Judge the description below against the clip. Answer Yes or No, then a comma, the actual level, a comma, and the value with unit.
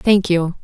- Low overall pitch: No, medium, 180 Hz